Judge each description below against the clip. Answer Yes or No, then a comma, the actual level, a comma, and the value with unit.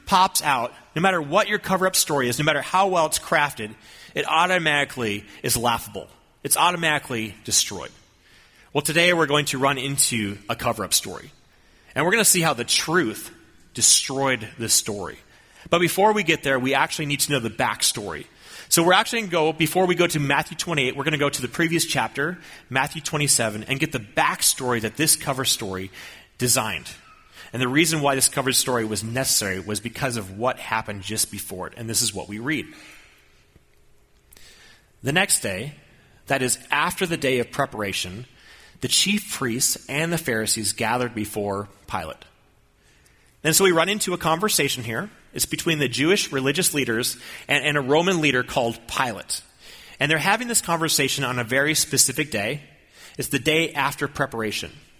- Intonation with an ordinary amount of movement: No, wide, 5.9 semitones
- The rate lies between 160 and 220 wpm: Yes, average, 180 wpm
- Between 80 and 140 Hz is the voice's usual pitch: Yes, low, 135 Hz